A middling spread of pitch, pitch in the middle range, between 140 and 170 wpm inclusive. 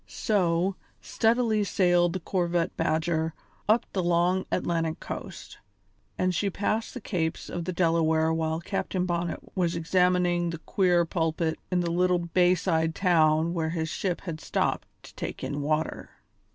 No: narrow, 2.1 semitones; medium, 175 Hz; average, 150 wpm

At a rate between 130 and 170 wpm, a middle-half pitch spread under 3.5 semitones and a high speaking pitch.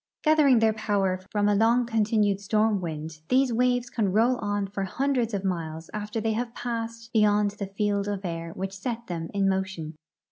No: average, 185 wpm; average, 3.1 semitones; high, 210 Hz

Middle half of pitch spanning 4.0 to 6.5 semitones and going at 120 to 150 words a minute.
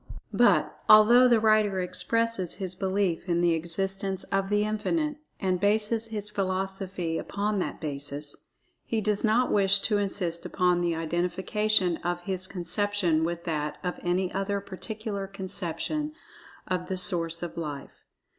No: average, 3.1 semitones; average, 145 wpm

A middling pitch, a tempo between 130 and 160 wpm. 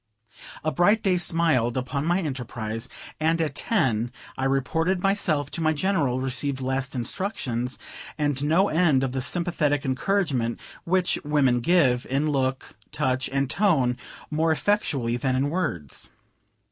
Yes: medium, 145 Hz; average, 140 wpm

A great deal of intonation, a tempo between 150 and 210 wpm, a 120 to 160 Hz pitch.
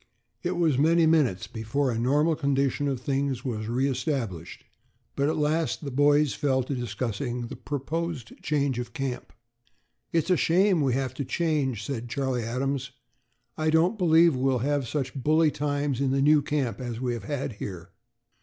No: average, 3.4 semitones; average, 175 wpm; medium, 140 Hz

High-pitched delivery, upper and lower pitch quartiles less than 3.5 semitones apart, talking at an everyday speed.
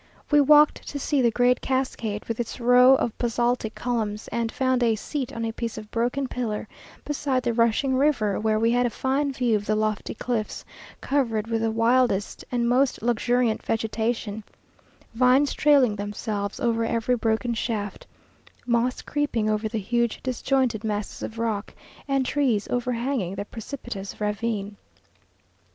Yes: high, 235 Hz; narrow, 2.6 semitones; average, 155 wpm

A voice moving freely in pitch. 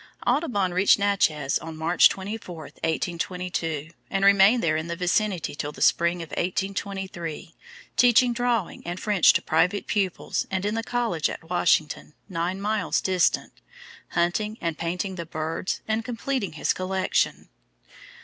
No: average, 3.5 semitones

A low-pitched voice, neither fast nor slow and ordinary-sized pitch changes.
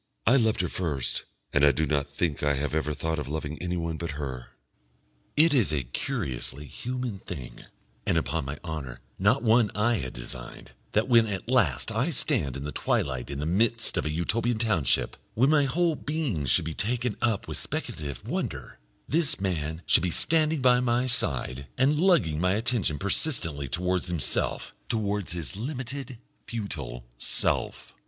No: very low, 90 Hz; average, 170 wpm; wide, 8.8 semitones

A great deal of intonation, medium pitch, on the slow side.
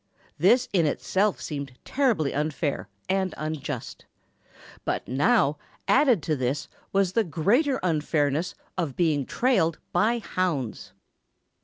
Yes: wide, 6.1 semitones; medium, 165 Hz; slow, 115 wpm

